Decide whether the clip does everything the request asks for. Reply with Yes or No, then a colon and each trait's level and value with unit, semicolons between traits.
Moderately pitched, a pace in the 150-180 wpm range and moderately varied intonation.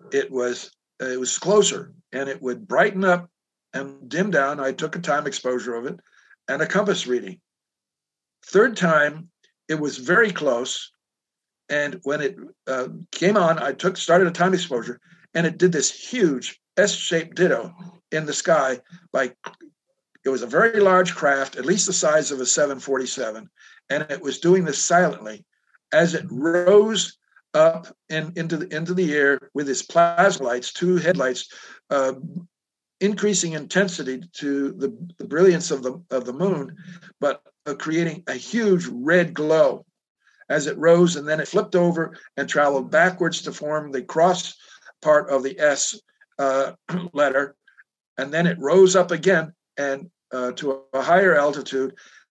Yes: medium, 165 Hz; average, 165 wpm; average, 4.8 semitones